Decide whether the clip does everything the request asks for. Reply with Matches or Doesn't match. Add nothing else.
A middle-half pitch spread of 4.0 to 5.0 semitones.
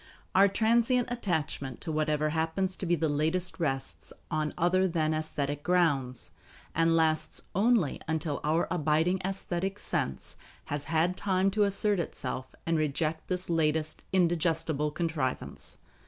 Doesn't match